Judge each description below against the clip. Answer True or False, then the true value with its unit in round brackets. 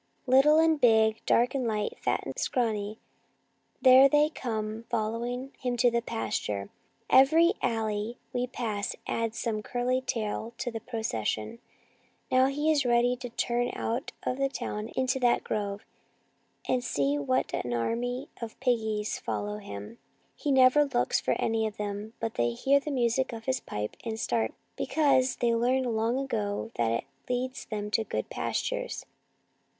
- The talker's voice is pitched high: True (235 Hz)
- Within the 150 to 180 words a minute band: True (160 wpm)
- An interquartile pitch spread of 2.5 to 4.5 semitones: True (3.2 semitones)